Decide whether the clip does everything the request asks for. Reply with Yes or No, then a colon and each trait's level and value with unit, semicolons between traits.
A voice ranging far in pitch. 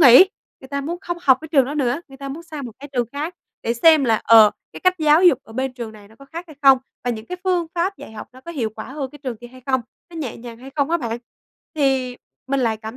No: average, 4.4 semitones